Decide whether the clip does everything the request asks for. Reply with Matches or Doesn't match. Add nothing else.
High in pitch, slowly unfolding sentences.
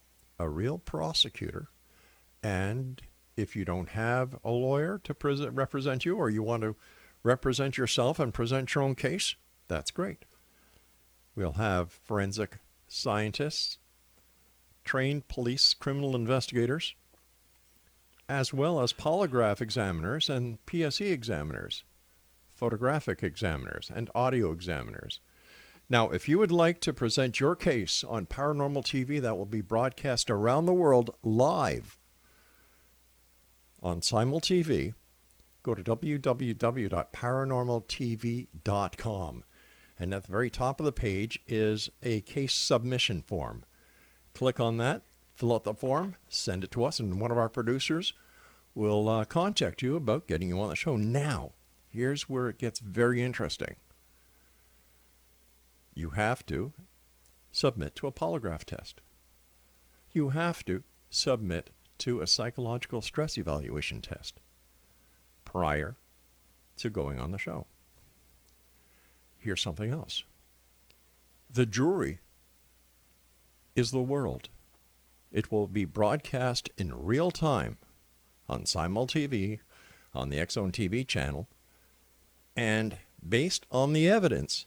Doesn't match